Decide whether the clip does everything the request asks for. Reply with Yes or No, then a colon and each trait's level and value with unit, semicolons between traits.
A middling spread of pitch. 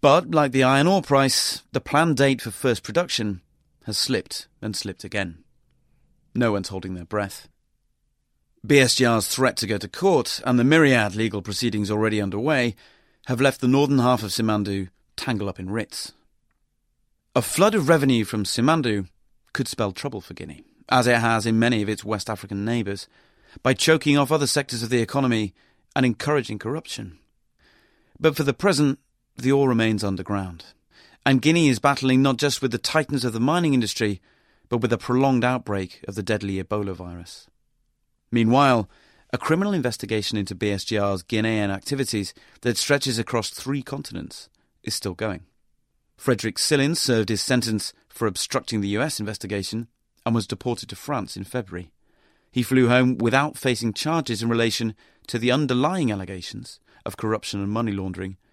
Yes: average, 4.5 semitones